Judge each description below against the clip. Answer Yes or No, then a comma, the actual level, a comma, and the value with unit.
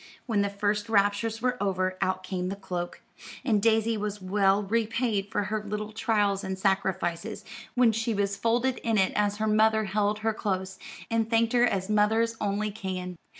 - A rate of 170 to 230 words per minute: Yes, average, 180 wpm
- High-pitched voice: Yes, high, 210 Hz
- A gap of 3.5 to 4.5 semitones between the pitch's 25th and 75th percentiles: No, narrow, 2.4 semitones